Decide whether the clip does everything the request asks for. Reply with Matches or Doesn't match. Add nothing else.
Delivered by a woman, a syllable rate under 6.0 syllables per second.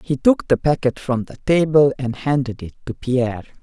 Matches